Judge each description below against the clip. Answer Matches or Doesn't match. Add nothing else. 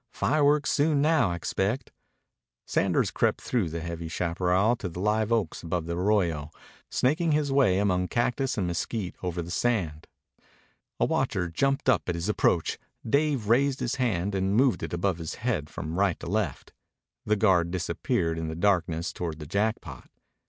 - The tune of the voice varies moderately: Doesn't match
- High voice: Doesn't match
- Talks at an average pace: Matches